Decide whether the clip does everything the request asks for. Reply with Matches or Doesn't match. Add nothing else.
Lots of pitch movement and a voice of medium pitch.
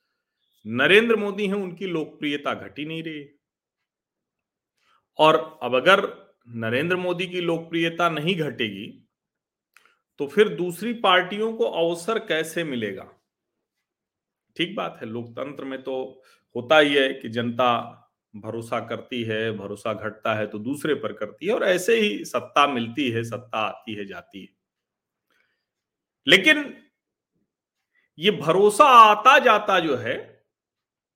Matches